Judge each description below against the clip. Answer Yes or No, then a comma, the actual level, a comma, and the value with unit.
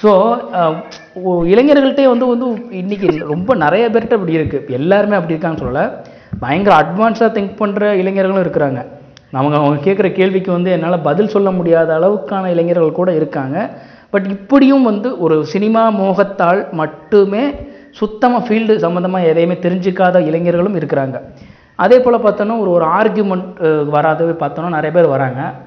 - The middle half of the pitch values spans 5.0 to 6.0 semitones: No, average, 4.5 semitones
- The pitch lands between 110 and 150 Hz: No, medium, 185 Hz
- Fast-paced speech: Yes, fast, 135 wpm